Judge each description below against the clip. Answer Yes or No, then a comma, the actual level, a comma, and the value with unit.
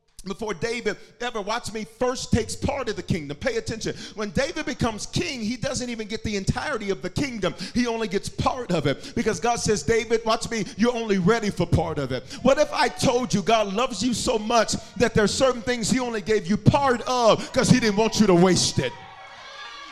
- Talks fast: Yes, fast, 225 wpm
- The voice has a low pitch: No, high, 225 Hz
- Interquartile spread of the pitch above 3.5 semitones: No, average, 3.2 semitones